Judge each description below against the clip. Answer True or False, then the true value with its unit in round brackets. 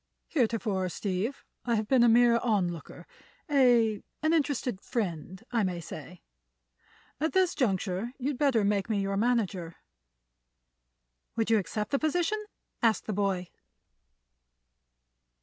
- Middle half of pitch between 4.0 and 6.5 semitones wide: True (4.5 semitones)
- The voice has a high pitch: True (220 Hz)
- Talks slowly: True (120 wpm)